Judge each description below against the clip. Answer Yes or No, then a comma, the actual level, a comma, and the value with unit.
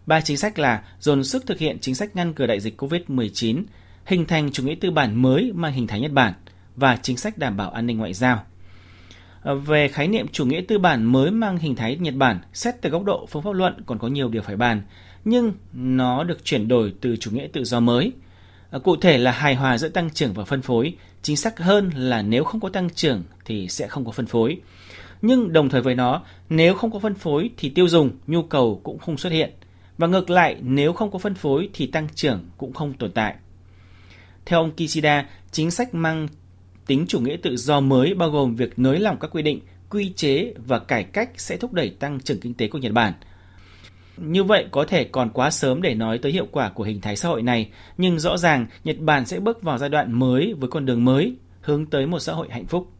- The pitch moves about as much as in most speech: No, wide, 6.3 semitones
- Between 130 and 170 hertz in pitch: Yes, low, 135 Hz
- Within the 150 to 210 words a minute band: No, average, 235 wpm